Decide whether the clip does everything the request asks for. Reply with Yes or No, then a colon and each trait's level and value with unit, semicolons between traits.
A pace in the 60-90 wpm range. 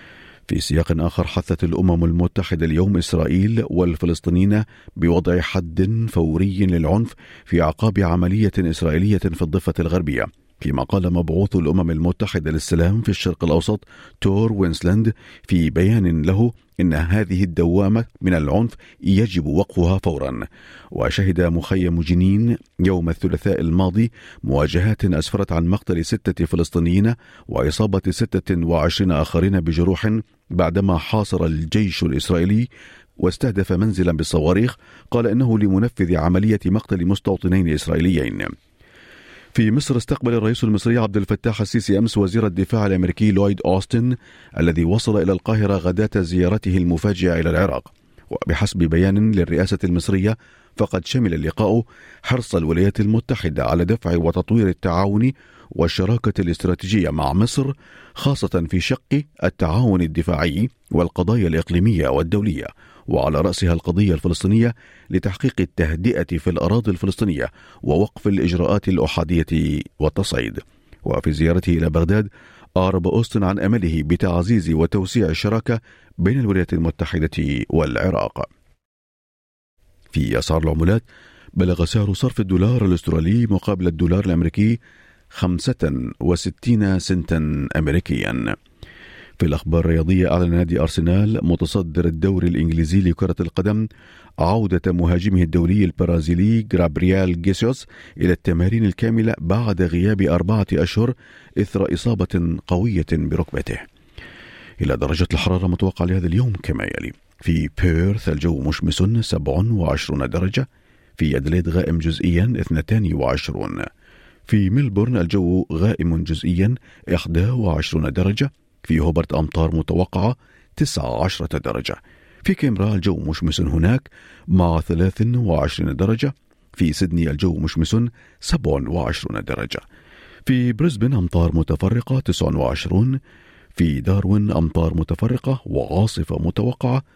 No: average, 110 wpm